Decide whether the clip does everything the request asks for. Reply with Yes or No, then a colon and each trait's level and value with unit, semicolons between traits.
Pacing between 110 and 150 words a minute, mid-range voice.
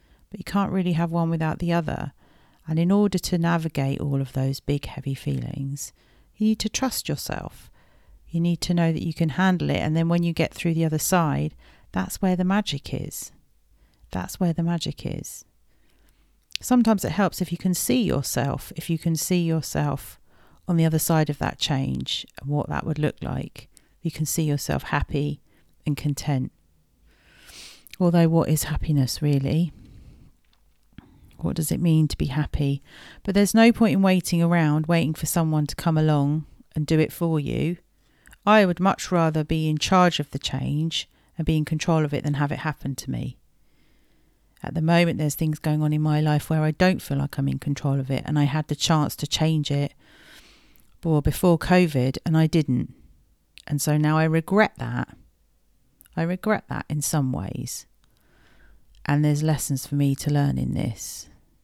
No: average, 185 wpm; medium, 155 Hz